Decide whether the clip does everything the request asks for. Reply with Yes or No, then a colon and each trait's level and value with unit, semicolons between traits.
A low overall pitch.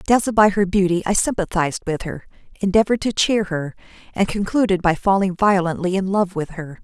No: high, 190 Hz